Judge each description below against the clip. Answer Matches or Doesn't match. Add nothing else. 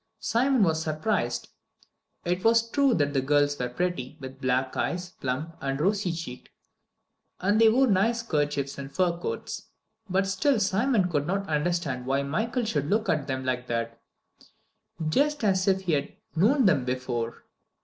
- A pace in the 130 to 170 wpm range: Matches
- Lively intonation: Matches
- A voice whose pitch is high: Doesn't match